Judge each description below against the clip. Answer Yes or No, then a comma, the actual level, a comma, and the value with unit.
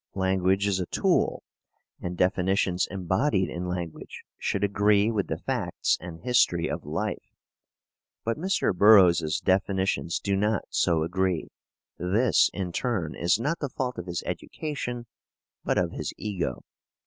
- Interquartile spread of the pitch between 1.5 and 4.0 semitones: Yes, average, 3.3 semitones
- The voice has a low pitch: Yes, very low, 95 Hz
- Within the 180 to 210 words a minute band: No, average, 140 wpm